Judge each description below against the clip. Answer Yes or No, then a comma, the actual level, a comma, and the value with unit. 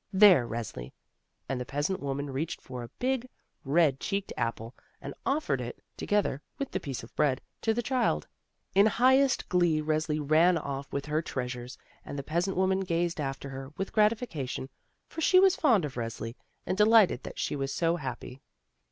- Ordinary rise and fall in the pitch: No, wide, 6.8 semitones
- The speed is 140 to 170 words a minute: No, average, 185 wpm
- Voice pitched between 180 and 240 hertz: No, medium, 155 Hz